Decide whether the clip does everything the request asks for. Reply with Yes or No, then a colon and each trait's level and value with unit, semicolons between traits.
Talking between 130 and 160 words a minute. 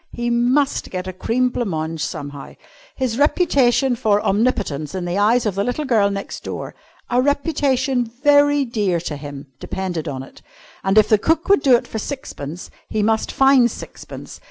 No: average, 175 wpm